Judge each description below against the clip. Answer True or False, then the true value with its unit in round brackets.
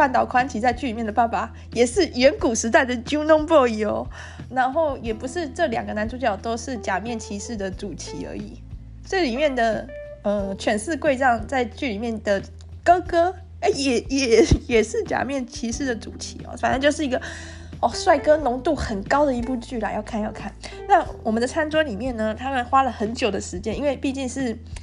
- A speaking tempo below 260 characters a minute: False (295 characters per minute)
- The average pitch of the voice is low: False (250 Hz)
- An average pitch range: True (5.0 semitones)